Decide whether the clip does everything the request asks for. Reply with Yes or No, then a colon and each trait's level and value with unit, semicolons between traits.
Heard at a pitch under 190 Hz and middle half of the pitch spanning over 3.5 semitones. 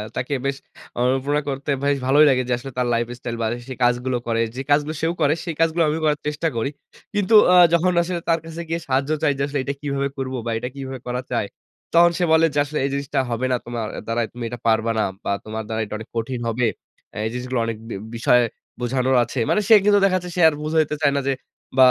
Yes: low, 135 Hz; average, 3.9 semitones